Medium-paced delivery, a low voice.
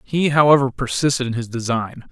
Yes: average, 170 wpm; low, 130 Hz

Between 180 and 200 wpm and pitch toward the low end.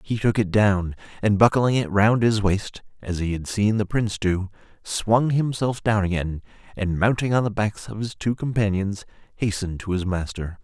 Yes: average, 190 wpm; low, 105 Hz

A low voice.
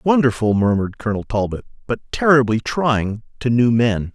Yes: low, 120 Hz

